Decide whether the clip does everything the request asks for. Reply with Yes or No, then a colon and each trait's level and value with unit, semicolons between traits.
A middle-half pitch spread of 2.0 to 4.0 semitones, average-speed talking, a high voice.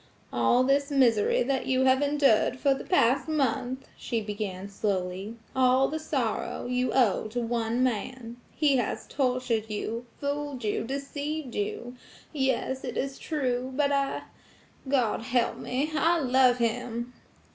No: average, 3.1 semitones; slow, 130 wpm; very high, 255 Hz